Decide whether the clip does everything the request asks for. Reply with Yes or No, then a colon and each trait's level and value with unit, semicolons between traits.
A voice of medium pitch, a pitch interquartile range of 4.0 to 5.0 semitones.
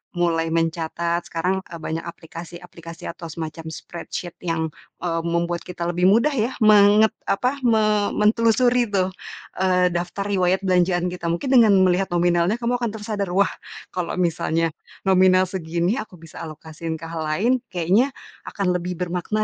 No: medium, 180 Hz; average, 3.4 semitones